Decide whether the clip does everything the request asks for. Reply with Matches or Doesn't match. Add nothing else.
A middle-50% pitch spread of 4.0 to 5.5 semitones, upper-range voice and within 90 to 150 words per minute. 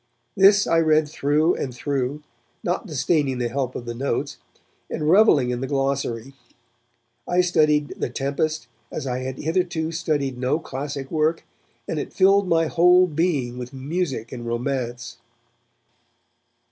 Doesn't match